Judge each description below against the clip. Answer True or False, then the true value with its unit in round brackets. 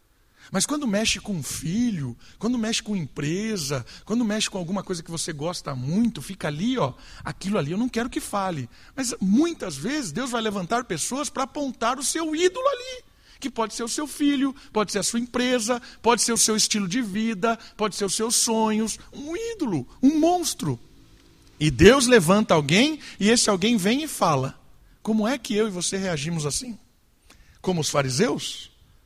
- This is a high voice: True (220 Hz)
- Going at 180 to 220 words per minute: True (185 wpm)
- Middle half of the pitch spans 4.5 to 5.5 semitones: True (5.2 semitones)